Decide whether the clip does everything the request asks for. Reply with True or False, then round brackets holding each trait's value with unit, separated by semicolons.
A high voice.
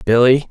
False (125 Hz)